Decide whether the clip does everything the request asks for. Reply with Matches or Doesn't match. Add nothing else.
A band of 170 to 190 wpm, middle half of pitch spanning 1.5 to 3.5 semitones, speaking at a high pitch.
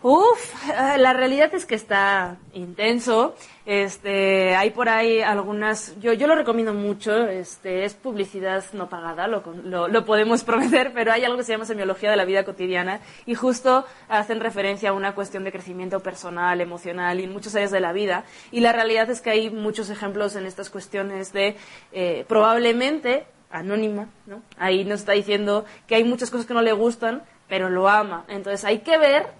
Matches